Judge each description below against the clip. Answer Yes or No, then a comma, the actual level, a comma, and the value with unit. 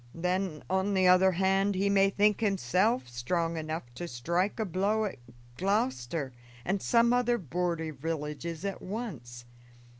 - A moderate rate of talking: Yes, average, 145 wpm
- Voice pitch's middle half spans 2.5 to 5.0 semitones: Yes, average, 3.8 semitones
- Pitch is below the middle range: No, medium, 185 Hz